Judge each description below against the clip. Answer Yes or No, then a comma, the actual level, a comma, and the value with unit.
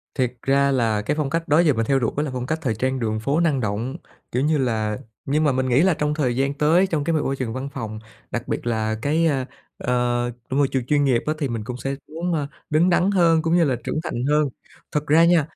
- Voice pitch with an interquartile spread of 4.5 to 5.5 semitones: No, average, 4.1 semitones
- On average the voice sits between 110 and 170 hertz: Yes, low, 135 Hz